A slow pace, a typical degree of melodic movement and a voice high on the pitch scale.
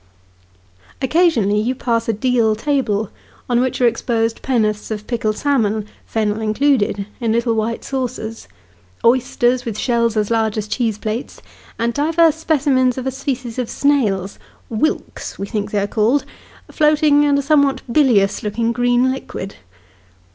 No: average, 145 wpm; average, 3.6 semitones; high, 235 Hz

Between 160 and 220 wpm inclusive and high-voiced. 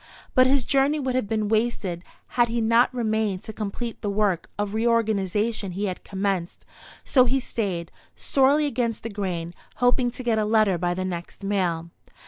Yes: average, 175 wpm; high, 215 Hz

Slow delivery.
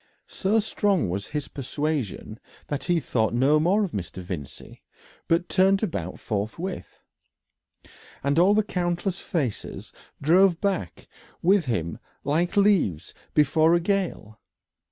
Yes: slow, 125 wpm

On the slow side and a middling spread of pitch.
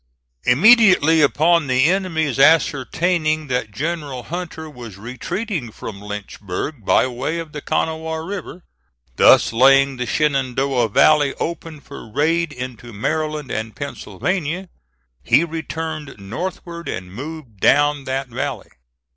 Yes: slow, 120 wpm; average, 4.5 semitones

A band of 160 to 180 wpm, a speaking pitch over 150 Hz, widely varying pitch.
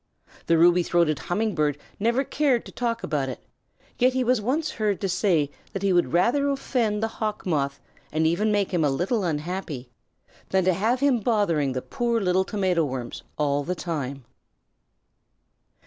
Yes: average, 175 wpm; medium, 185 Hz; wide, 6.5 semitones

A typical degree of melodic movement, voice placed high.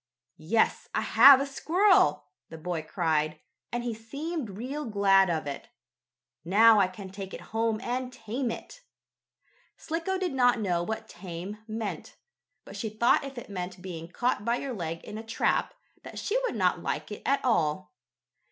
No: wide, 5.8 semitones; high, 220 Hz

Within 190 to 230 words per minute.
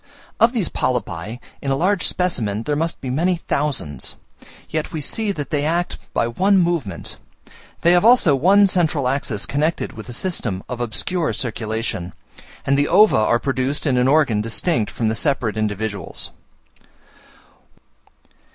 No: average, 150 wpm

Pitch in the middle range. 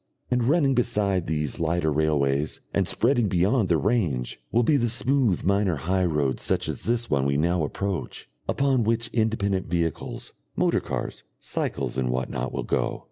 No: very low, 95 Hz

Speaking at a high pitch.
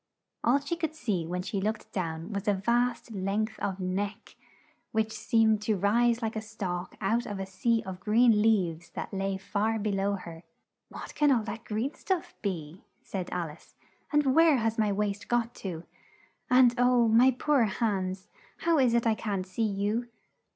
Yes: high, 215 Hz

